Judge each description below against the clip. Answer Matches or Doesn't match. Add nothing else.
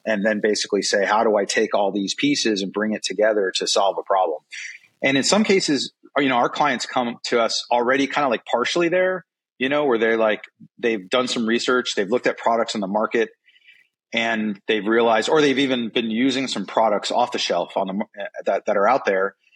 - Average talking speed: Doesn't match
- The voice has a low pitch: Matches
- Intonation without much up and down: Doesn't match